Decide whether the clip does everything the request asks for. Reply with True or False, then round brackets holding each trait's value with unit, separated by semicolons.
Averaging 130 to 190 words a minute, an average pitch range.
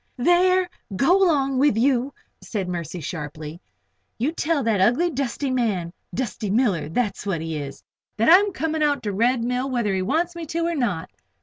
False (185 wpm; 8.2 semitones)